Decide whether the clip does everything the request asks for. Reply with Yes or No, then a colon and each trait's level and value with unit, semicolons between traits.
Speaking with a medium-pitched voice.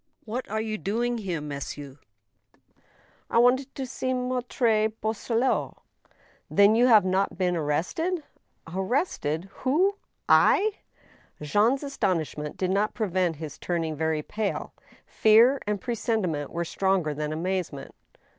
No: high, 200 Hz